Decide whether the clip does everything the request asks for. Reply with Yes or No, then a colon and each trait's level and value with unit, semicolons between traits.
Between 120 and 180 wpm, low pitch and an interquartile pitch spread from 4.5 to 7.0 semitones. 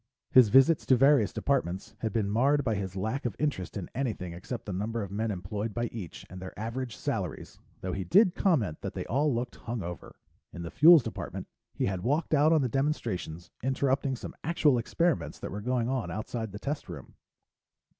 No: average, 200 wpm; low, 115 Hz; wide, 5.6 semitones